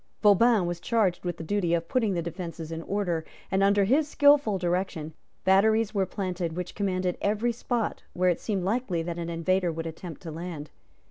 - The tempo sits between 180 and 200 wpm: Yes, average, 190 wpm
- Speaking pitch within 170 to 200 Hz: Yes, medium, 185 Hz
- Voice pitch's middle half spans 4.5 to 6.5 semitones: No, average, 3.3 semitones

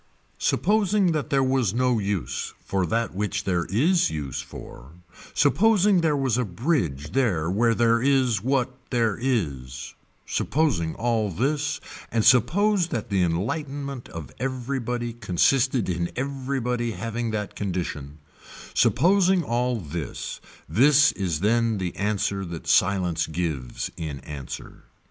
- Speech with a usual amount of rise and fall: No, wide, 7.1 semitones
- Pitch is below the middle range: Yes, low, 115 Hz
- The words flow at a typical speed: No, slow, 130 wpm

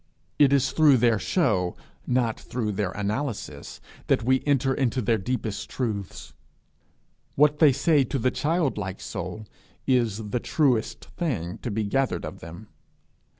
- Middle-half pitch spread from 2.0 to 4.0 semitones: No, average, 4.7 semitones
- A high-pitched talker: No, low, 120 Hz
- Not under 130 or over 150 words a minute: Yes, average, 145 wpm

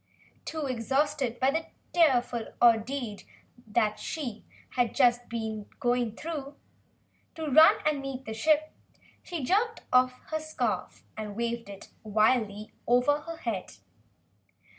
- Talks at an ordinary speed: No, slow, 120 wpm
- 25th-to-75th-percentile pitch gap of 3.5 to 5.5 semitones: Yes, average, 4.7 semitones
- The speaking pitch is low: No, very high, 255 Hz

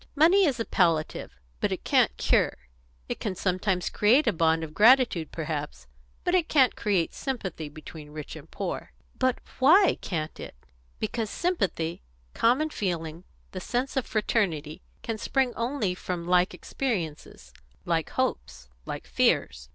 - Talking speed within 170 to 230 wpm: No, average, 145 wpm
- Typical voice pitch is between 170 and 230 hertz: Yes, high, 190 Hz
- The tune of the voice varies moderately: No, wide, 7.9 semitones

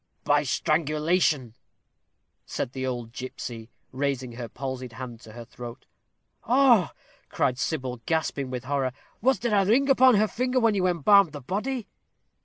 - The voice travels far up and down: Yes, wide, 8.2 semitones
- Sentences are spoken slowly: No, average, 150 wpm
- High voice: No, medium, 145 Hz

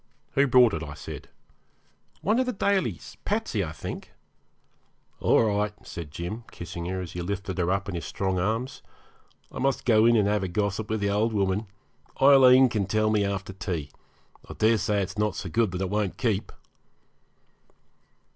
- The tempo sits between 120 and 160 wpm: No, average, 185 wpm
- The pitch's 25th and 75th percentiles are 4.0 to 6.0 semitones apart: No, average, 3.3 semitones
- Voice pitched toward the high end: No, low, 105 Hz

